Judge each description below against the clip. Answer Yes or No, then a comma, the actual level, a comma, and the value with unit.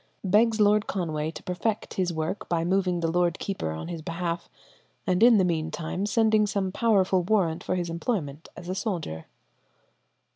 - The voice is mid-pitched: Yes, medium, 180 Hz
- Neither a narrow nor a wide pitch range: Yes, average, 3.6 semitones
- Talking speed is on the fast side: No, average, 175 wpm